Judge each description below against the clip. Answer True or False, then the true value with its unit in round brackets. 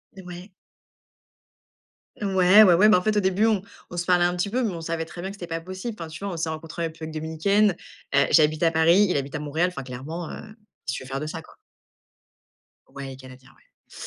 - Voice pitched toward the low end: False (170 Hz)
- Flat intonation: False (3.2 semitones)